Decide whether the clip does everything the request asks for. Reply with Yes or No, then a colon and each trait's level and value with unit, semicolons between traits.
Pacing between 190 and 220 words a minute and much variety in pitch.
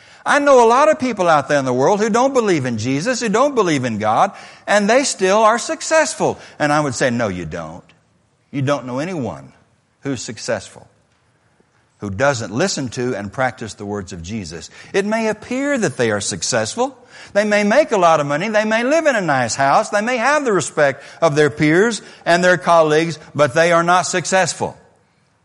Yes: fast, 205 wpm; wide, 8.4 semitones